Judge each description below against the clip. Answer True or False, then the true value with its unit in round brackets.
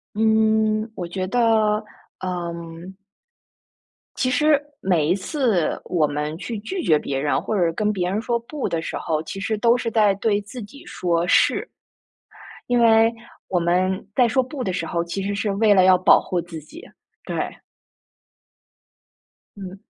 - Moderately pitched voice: False (200 Hz)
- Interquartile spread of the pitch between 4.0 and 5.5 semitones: True (4.4 semitones)